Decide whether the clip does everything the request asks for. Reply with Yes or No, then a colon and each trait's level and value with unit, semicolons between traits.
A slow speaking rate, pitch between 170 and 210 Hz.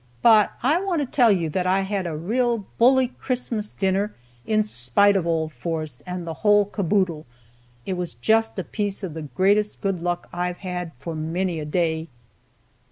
No: average, 180 wpm; medium, 185 Hz